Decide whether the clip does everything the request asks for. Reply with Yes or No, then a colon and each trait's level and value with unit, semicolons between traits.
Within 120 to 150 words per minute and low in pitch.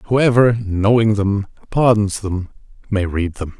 Yes: slow, 135 wpm; low, 105 Hz